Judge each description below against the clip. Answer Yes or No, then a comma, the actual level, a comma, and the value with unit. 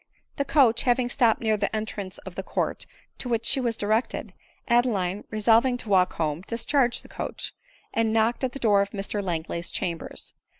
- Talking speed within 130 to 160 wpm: No, average, 180 wpm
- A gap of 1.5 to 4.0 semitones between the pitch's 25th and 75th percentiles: Yes, average, 3.3 semitones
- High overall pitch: Yes, high, 220 Hz